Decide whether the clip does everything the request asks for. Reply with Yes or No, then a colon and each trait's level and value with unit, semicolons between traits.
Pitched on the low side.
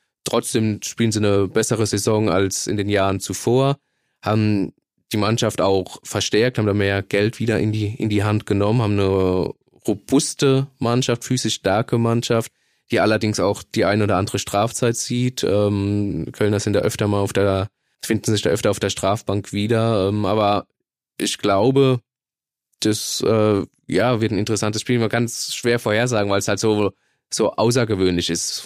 Yes: low, 105 Hz